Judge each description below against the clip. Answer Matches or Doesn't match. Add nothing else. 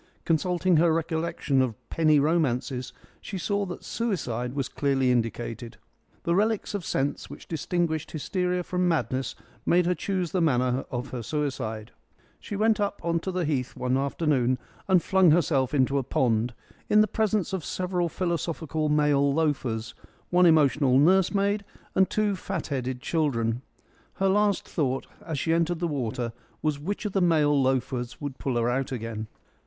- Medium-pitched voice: Matches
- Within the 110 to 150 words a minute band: Doesn't match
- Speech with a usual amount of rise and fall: Doesn't match